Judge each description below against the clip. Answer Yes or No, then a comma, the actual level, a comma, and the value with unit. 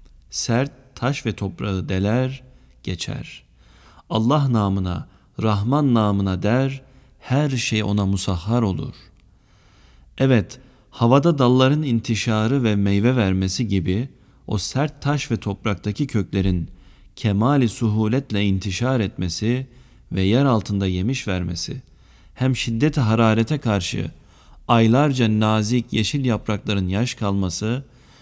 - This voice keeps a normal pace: Yes, average, 105 wpm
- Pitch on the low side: Yes, low, 110 Hz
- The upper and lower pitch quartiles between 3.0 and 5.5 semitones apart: Yes, average, 4.5 semitones